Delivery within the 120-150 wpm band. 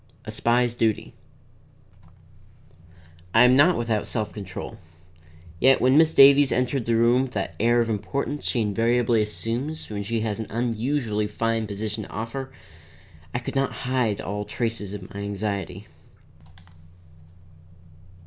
Yes: average, 140 wpm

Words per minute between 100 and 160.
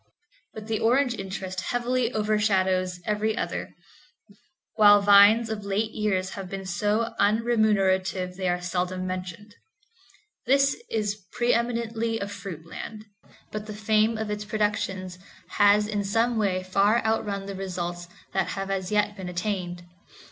Yes: average, 140 wpm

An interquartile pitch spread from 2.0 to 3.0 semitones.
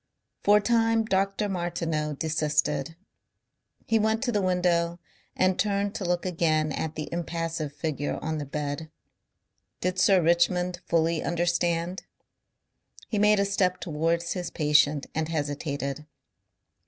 No: average, 3.4 semitones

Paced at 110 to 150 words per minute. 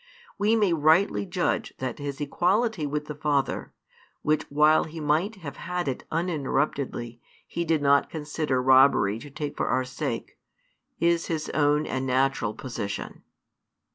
Yes: average, 145 wpm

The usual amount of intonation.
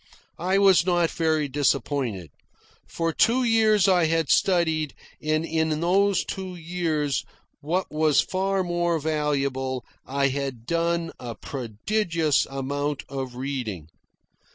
Yes: average, 4.1 semitones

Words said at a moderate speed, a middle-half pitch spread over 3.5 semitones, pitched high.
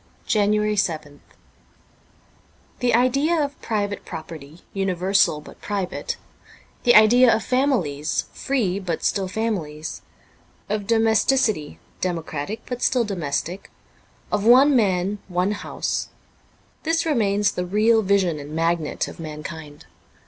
No: slow, 120 wpm; wide, 5.4 semitones; high, 200 Hz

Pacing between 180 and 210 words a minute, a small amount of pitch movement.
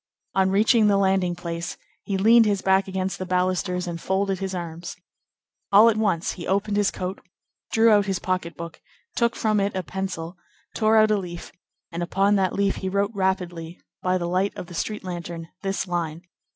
Yes: average, 195 wpm; narrow, 2.3 semitones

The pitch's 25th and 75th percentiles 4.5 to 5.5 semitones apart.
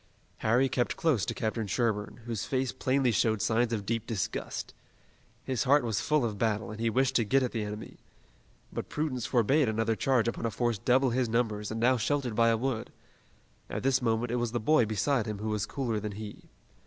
No: average, 2.8 semitones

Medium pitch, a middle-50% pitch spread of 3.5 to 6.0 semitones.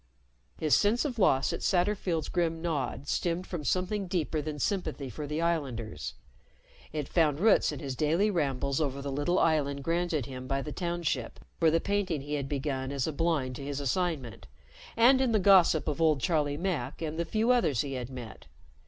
Yes: medium, 155 Hz; average, 4.1 semitones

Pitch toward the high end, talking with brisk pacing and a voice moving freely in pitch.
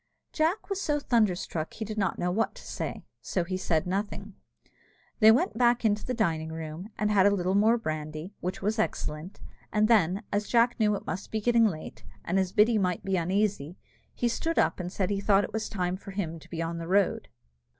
No: high, 200 Hz; fast, 220 wpm; average, 3.6 semitones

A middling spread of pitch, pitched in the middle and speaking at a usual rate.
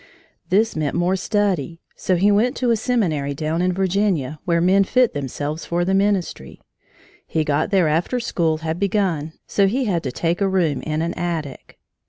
Yes: average, 4.2 semitones; medium, 175 Hz; average, 185 wpm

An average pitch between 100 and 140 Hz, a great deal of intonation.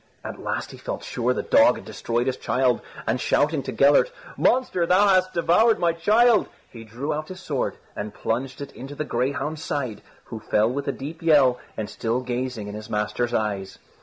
Yes: low, 135 Hz; wide, 5.8 semitones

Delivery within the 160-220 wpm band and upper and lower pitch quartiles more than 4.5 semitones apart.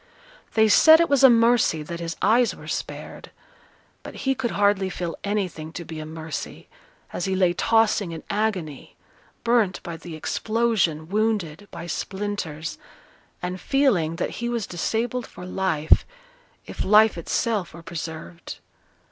No: average, 150 wpm; average, 5.2 semitones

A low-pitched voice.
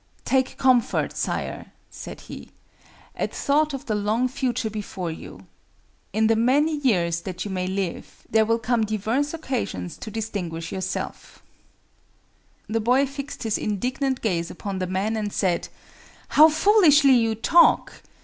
No: high, 225 Hz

